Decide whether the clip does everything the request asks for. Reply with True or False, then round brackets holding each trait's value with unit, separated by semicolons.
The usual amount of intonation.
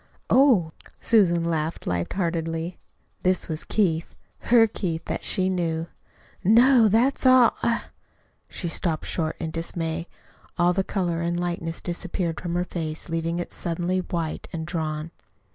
False (2.3 semitones)